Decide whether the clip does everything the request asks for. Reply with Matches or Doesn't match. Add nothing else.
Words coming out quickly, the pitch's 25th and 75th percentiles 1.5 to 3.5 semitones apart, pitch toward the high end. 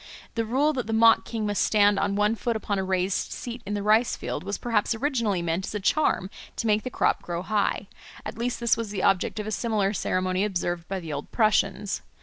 Matches